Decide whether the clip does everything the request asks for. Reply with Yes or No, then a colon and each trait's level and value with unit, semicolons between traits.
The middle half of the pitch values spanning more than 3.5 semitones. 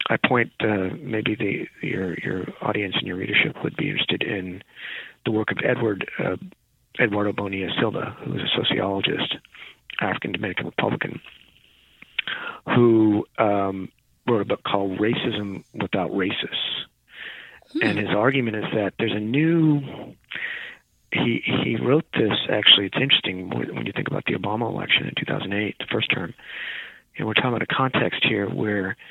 No: average, 2.8 semitones